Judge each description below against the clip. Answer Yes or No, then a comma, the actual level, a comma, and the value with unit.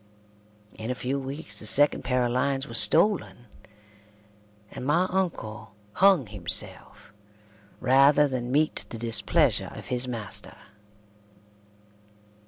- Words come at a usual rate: No, slow, 115 wpm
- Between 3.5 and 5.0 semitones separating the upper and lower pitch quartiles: Yes, average, 4.1 semitones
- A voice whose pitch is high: No, low, 125 Hz